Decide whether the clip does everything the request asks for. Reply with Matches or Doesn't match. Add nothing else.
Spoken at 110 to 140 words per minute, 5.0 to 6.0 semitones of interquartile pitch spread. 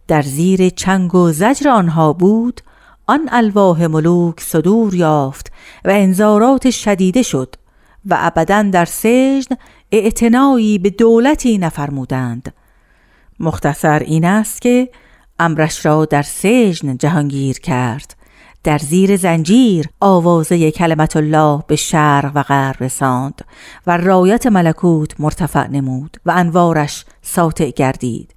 Matches